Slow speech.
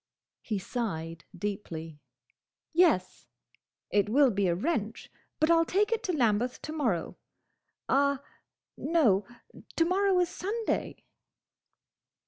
Yes: slow, 110 wpm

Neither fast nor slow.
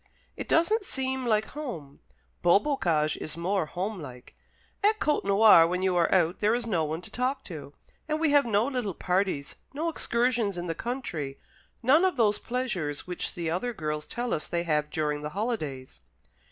Yes: average, 180 wpm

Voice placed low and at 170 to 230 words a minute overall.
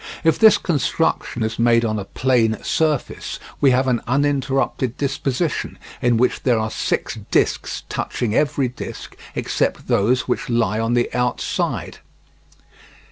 No: low, 125 Hz; slow, 135 wpm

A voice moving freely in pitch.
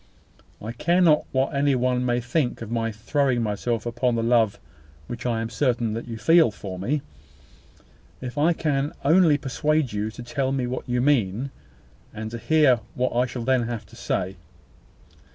No: average, 3.4 semitones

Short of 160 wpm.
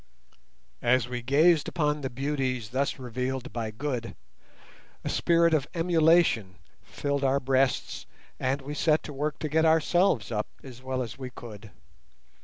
Yes: average, 150 wpm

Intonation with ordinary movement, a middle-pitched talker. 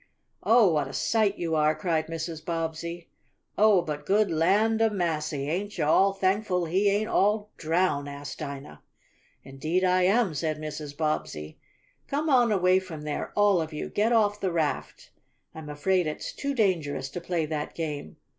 Yes: average, 4.7 semitones; medium, 170 Hz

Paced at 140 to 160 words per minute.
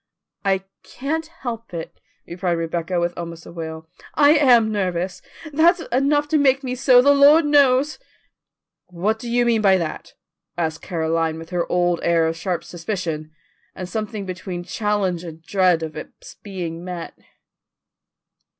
Yes: average, 150 wpm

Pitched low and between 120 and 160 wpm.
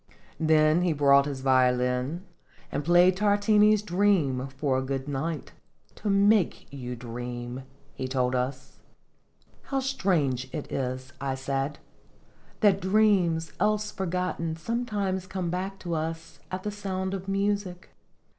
No: medium, 165 Hz; average, 140 wpm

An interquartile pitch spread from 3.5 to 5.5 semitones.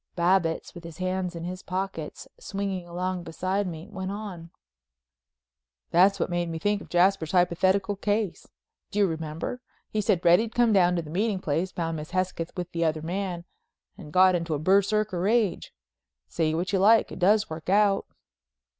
No: average, 2.7 semitones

